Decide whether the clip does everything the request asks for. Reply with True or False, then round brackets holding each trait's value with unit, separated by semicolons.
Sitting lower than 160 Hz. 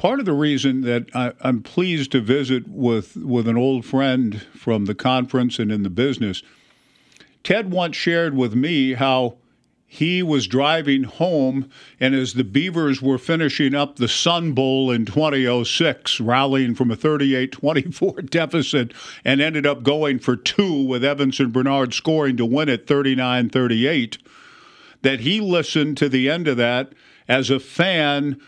True (135 Hz)